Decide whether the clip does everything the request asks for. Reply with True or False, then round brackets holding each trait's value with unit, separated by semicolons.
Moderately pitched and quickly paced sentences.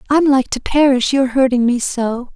False (260 Hz; 255 wpm)